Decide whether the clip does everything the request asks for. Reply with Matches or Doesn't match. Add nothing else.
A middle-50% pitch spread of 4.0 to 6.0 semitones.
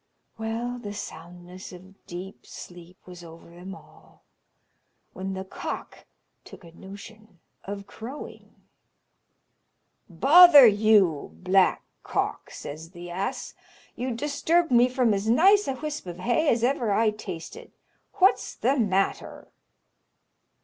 Matches